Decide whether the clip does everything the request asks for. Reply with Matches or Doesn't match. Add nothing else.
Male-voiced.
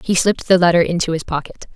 Doesn't match